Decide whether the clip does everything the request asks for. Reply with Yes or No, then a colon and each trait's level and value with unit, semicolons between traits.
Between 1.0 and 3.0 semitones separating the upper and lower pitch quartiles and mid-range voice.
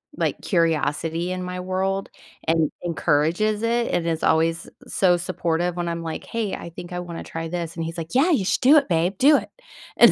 Yes: narrow, 2.6 semitones; medium, 175 Hz